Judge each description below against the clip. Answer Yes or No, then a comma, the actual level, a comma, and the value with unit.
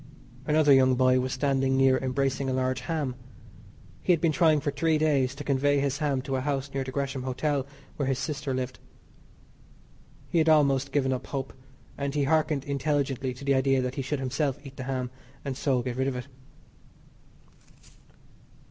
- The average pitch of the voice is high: No, low, 135 Hz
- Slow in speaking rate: No, average, 185 wpm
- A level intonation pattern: Yes, narrow, 1.7 semitones